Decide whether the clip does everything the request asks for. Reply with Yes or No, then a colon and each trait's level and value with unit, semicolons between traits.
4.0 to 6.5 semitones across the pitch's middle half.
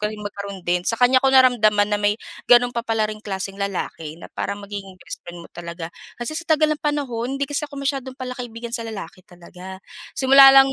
Yes: average, 4.8 semitones